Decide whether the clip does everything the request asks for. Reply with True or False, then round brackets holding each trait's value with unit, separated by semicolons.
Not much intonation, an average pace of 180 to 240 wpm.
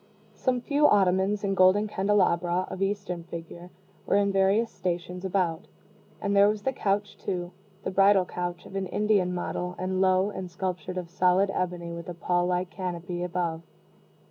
False (2.0 semitones; 170 wpm)